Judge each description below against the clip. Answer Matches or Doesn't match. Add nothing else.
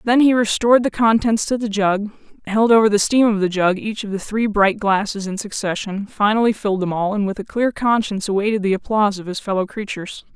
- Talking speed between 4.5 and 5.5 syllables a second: Doesn't match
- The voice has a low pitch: Doesn't match